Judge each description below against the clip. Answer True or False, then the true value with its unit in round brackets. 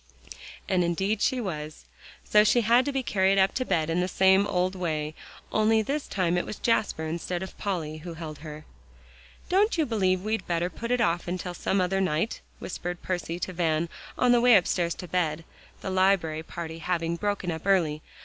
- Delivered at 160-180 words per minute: False (195 wpm)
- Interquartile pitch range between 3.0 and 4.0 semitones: True (3.6 semitones)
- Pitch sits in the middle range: True (180 Hz)